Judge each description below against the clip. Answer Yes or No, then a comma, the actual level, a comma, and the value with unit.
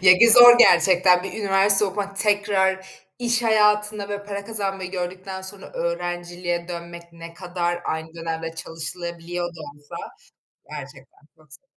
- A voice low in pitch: No, medium, 185 Hz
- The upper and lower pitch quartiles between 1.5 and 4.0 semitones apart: Yes, average, 2.8 semitones